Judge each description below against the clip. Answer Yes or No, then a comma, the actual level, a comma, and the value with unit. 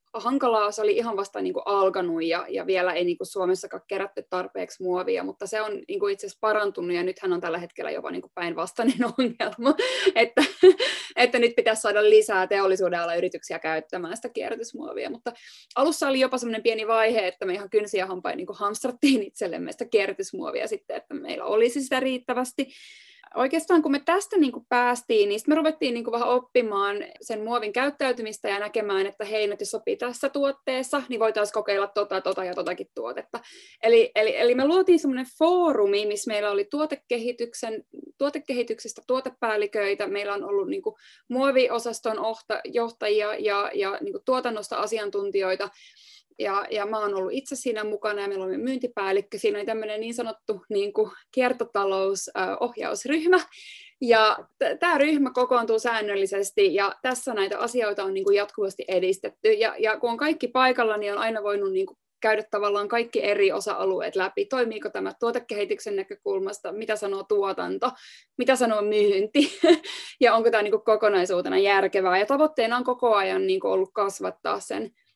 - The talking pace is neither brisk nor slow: No, fast, 165 wpm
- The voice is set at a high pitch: Yes, high, 230 Hz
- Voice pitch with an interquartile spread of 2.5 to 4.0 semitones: No, average, 5.3 semitones